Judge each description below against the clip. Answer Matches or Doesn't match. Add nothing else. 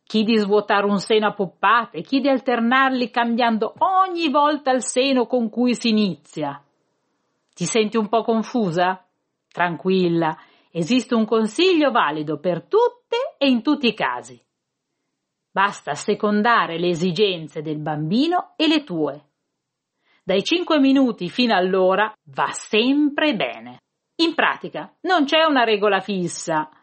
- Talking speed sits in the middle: Matches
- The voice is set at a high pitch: Matches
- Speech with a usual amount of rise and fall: Doesn't match